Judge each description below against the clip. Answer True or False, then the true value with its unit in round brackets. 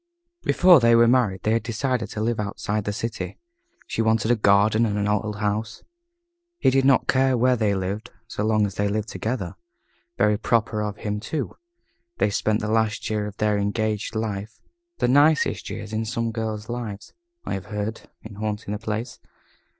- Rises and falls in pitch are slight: True (1.8 semitones)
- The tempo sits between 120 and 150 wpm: False (185 wpm)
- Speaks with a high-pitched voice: False (110 Hz)